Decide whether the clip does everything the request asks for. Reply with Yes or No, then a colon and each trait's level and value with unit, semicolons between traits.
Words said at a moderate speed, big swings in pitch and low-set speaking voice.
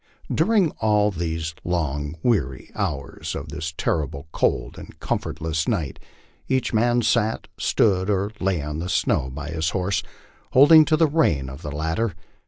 Yes: average, 155 wpm; wide, 6.3 semitones; very low, 85 Hz